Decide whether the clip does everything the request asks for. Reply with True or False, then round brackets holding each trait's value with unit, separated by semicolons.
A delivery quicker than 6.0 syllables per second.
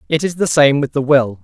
False (5.6 syllables/s)